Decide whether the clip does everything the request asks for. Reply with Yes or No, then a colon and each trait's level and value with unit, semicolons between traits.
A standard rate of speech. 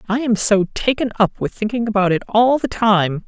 No: fast, 220 wpm